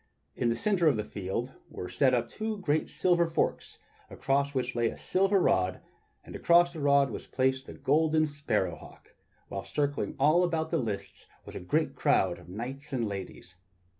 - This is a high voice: No, medium, 140 Hz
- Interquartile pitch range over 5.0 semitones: Yes, wide, 5.5 semitones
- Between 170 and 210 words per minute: Yes, average, 180 wpm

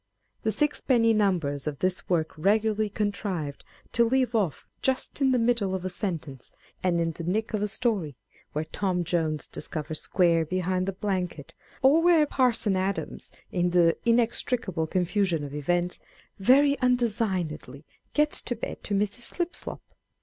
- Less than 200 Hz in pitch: Yes, high, 190 Hz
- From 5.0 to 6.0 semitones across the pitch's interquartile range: Yes, wide, 5.4 semitones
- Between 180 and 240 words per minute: No, average, 155 wpm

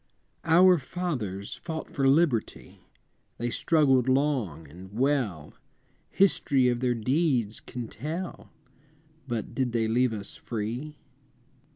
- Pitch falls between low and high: No, low, 125 Hz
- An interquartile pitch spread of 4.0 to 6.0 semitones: Yes, average, 5.2 semitones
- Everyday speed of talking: No, slow, 115 wpm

